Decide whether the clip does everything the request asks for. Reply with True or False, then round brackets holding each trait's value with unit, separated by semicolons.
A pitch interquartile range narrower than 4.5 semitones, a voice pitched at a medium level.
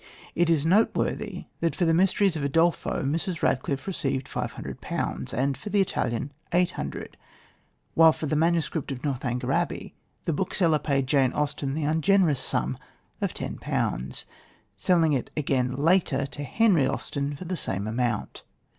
True (4.1 semitones; 150 Hz)